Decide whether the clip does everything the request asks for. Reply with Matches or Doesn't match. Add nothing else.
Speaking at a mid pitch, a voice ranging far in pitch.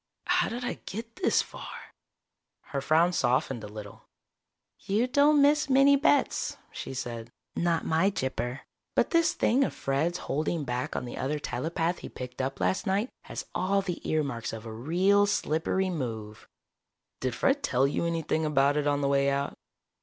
Matches